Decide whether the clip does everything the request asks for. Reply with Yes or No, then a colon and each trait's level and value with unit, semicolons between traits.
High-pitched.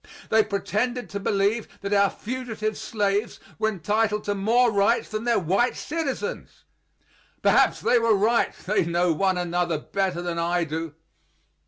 Yes: high, 205 Hz